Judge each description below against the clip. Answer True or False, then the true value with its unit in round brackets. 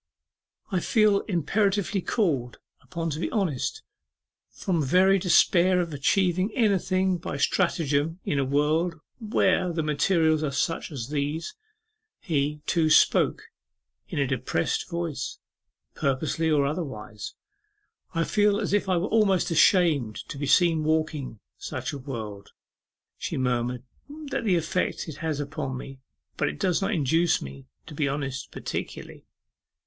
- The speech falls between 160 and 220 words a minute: False (140 wpm)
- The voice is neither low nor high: True (160 Hz)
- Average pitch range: True (4.8 semitones)